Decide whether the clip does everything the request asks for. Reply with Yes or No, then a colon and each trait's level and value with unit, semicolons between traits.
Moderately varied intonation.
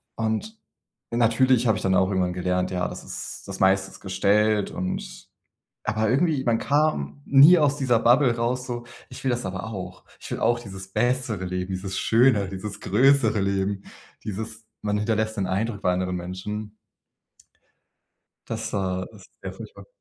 Yes: average, 4.2 semitones